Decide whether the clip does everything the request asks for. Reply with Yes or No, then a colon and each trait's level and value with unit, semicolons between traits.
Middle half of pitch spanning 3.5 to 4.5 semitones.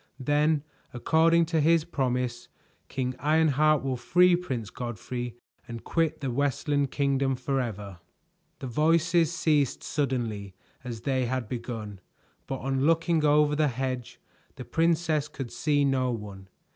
Yes: average, 4.0 semitones